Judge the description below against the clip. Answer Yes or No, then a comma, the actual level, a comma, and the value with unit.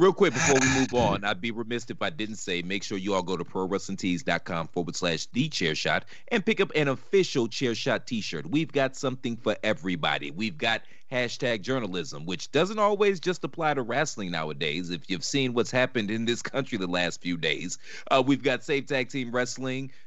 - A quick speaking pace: Yes, fast, 210 wpm